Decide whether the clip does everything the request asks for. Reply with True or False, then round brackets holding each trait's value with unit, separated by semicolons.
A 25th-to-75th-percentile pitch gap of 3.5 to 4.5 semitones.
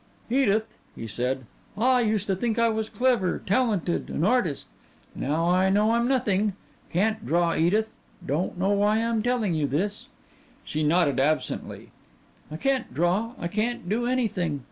False (5.1 semitones)